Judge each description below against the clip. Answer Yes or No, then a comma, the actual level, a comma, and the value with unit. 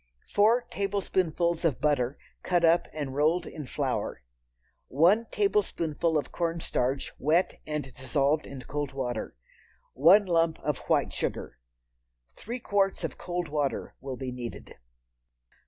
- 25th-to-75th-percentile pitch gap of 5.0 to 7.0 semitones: No, average, 4.4 semitones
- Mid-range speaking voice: Yes, medium, 155 Hz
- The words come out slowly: Yes, slow, 125 wpm